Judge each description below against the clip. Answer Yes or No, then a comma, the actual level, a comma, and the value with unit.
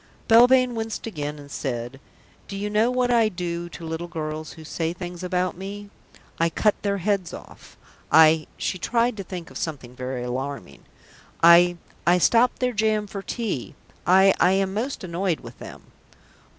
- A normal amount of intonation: Yes, average, 4.7 semitones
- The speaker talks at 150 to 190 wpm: Yes, average, 175 wpm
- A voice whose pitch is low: No, medium, 180 Hz